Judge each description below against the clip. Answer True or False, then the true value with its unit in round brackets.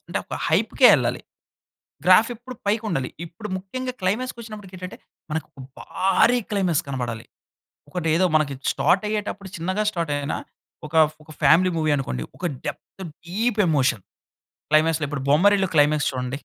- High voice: False (180 Hz)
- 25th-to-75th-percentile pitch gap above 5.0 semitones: True (5.4 semitones)